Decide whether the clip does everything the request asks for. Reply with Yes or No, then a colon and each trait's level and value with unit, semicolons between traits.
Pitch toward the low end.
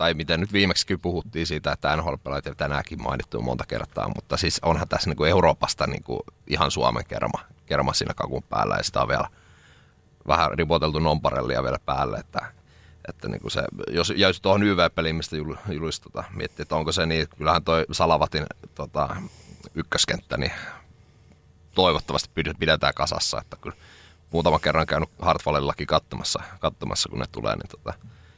Yes: very low, 80 Hz